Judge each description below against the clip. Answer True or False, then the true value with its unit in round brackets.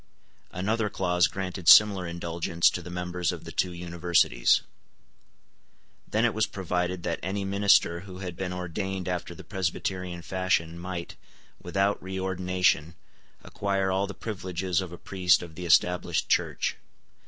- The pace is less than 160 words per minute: True (140 wpm)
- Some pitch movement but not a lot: False (1.7 semitones)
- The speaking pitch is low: True (90 Hz)